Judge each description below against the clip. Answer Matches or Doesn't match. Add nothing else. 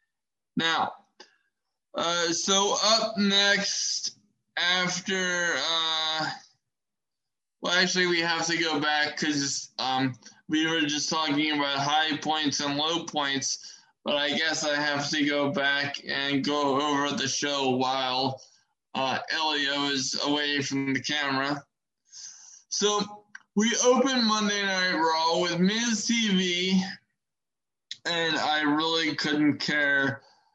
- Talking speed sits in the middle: Doesn't match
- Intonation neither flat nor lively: Matches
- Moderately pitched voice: Matches